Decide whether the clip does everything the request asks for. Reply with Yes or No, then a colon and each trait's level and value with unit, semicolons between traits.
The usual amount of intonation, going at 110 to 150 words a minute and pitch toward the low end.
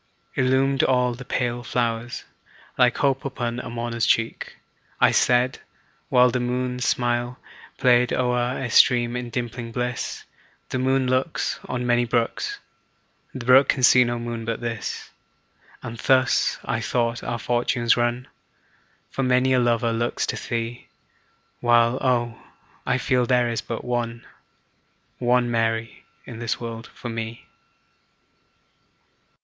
No: narrow, 1.2 semitones; slow, 135 wpm; low, 120 Hz